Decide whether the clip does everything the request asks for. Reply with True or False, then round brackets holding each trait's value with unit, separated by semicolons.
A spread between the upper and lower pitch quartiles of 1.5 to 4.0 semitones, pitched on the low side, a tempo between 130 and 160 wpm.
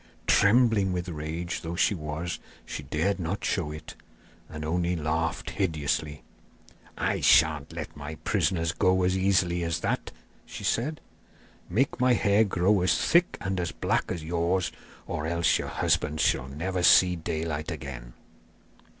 True (3.2 semitones; 85 Hz; 150 wpm)